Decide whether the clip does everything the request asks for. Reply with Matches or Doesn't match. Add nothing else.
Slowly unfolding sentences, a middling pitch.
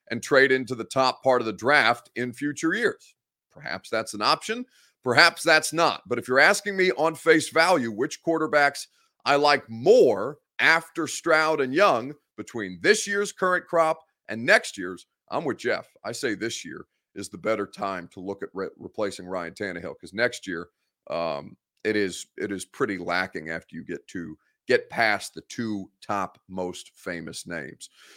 Doesn't match